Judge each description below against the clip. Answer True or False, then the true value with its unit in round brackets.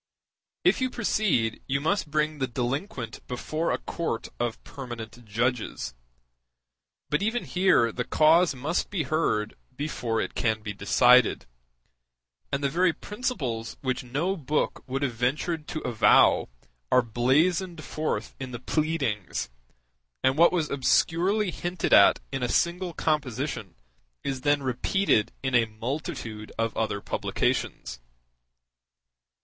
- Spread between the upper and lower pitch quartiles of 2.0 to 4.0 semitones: False (5.5 semitones)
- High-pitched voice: False (135 Hz)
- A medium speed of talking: False (130 wpm)